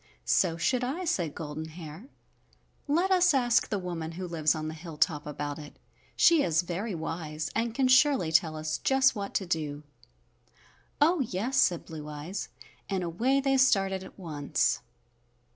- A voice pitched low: No, medium, 175 Hz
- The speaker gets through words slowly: No, average, 160 wpm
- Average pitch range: No, wide, 8.0 semitones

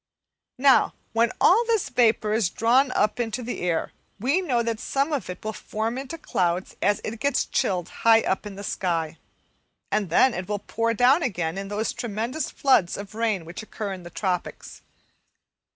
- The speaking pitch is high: Yes, high, 220 Hz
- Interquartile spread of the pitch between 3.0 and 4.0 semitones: No, average, 4.5 semitones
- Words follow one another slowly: No, average, 185 wpm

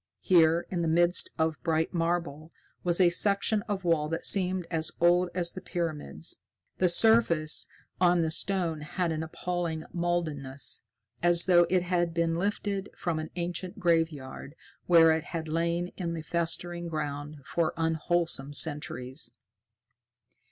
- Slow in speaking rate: No, average, 145 wpm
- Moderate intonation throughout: No, narrow, 1.8 semitones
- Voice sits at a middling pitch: Yes, medium, 170 Hz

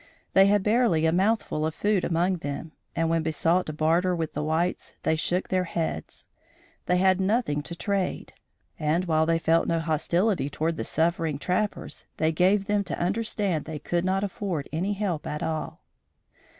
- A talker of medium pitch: Yes, medium, 170 Hz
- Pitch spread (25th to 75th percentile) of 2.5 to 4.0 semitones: Yes, average, 3.2 semitones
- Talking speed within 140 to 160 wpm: No, average, 175 wpm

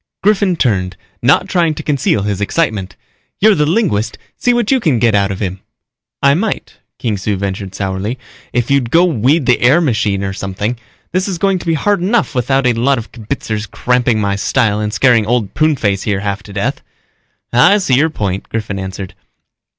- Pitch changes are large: Yes, wide, 7.6 semitones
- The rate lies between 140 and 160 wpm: No, average, 190 wpm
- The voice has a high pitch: No, low, 120 Hz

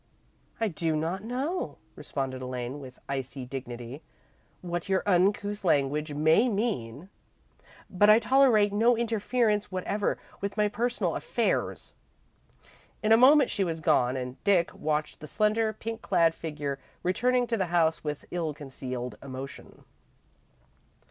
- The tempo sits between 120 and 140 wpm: Yes, slow, 135 wpm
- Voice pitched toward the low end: No, medium, 175 Hz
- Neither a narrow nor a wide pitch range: No, wide, 7.2 semitones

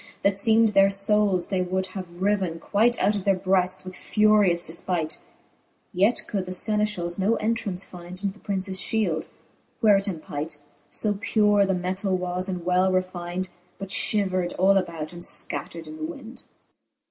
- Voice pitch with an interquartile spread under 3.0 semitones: Yes, narrow, 2.4 semitones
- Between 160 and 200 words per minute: Yes, average, 170 wpm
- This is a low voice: No, high, 190 Hz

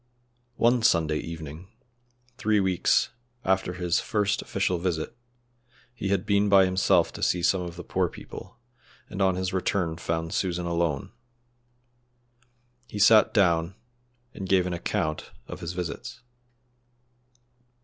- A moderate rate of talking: No, slow, 130 wpm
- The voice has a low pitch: Yes, very low, 90 Hz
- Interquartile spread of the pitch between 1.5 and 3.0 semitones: Yes, narrow, 2.5 semitones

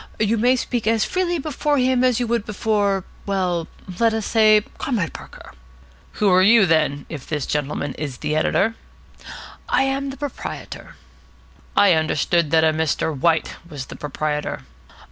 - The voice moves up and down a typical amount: No, wide, 7.0 semitones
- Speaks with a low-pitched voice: No, high, 200 Hz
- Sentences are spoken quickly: No, average, 160 wpm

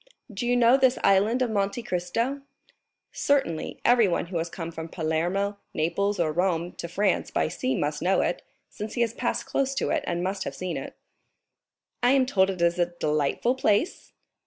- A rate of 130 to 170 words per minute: No, average, 185 wpm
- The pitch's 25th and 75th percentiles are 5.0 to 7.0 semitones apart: Yes, wide, 5.6 semitones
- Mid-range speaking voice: No, high, 195 Hz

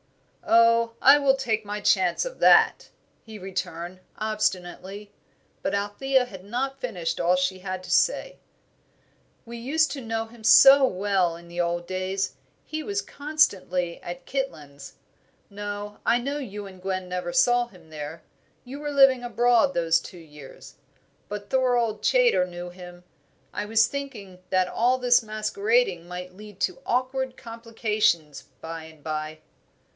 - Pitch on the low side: No, high, 210 Hz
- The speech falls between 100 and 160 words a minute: Yes, average, 150 wpm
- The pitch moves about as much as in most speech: No, wide, 5.7 semitones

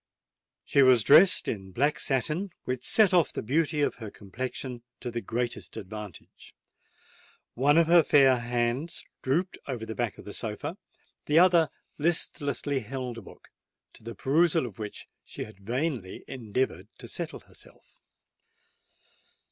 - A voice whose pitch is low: Yes, low, 130 Hz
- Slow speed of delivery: No, average, 150 wpm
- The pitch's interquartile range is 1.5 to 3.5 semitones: No, average, 4.7 semitones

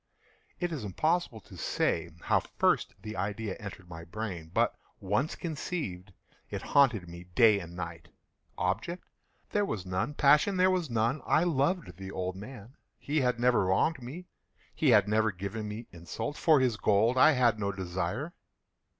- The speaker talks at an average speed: Yes, average, 165 wpm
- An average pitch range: No, wide, 7.1 semitones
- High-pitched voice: No, low, 110 Hz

